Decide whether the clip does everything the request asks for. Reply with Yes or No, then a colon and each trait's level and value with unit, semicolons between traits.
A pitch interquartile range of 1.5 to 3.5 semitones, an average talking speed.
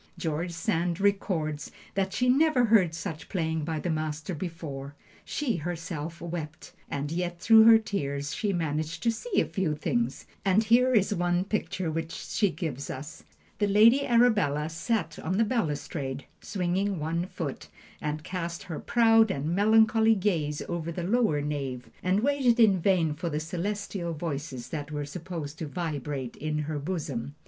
No: average, 5.1 semitones; average, 160 wpm